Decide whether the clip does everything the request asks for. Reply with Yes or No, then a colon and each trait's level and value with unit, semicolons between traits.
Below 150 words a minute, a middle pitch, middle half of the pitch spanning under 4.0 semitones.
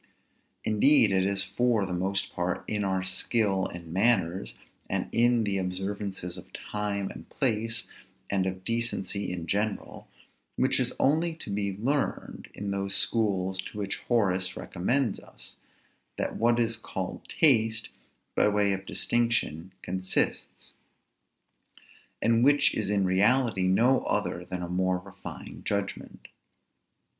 No: slow, 135 wpm; low, 100 Hz; average, 3.5 semitones